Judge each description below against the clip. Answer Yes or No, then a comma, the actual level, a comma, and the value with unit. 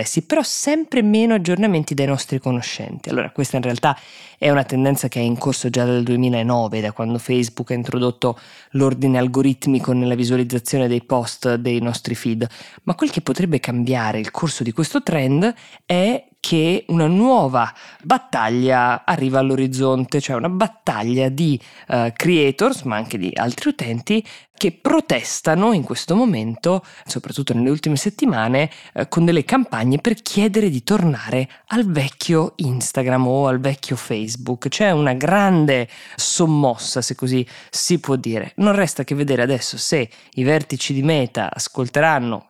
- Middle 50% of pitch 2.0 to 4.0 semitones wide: No, average, 5.3 semitones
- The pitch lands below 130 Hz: No, low, 135 Hz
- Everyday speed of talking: Yes, average, 150 wpm